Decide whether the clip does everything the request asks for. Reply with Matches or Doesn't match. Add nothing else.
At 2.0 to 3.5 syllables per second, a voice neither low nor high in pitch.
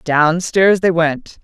Matches